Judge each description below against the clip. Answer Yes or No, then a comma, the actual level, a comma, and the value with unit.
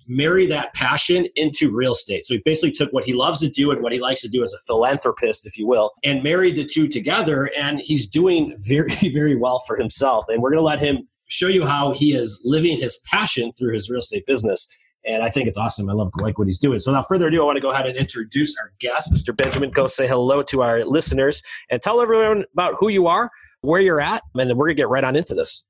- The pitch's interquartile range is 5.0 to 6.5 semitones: Yes, average, 5.3 semitones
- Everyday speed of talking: No, fast, 260 wpm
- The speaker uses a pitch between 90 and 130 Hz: No, medium, 140 Hz